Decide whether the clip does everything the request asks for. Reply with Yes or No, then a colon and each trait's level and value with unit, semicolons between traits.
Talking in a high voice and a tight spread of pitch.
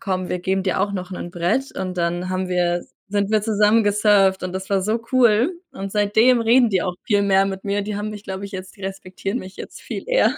Yes: high, 195 Hz; narrow, 2.2 semitones